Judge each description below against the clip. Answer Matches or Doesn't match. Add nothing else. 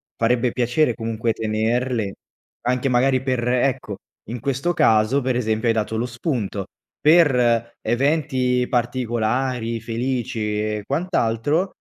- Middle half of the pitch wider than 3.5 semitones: Doesn't match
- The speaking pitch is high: Doesn't match